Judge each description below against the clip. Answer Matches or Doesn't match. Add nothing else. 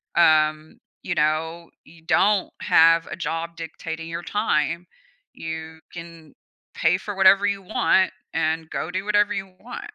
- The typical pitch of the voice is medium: Matches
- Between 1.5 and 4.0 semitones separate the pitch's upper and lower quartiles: Matches